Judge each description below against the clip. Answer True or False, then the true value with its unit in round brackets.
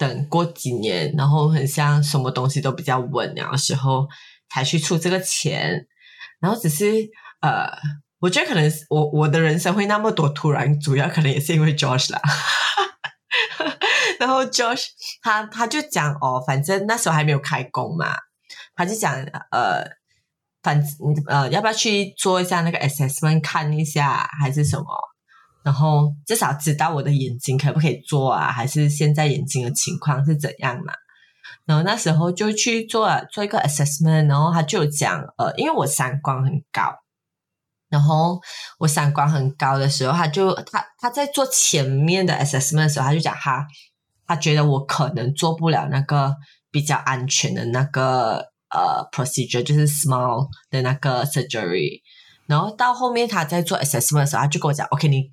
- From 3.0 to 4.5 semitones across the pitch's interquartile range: True (3.4 semitones)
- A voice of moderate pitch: True (150 Hz)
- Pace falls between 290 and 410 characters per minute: True (310 characters per minute)